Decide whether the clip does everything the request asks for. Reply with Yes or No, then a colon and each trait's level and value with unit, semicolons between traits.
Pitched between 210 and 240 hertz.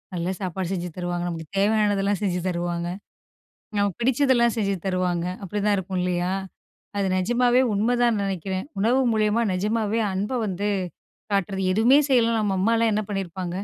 No: high, 200 Hz